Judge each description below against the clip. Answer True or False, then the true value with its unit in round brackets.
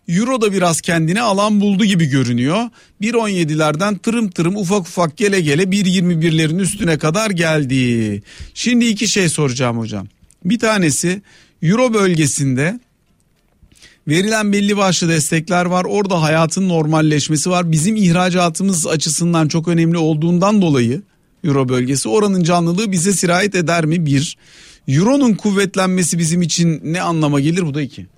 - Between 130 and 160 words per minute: True (135 wpm)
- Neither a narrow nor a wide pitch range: True (4.3 semitones)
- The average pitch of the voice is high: False (175 Hz)